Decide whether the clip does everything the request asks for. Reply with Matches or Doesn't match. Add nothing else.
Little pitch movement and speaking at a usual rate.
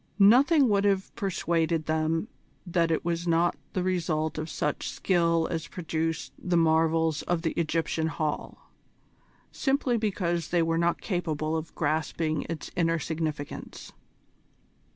Doesn't match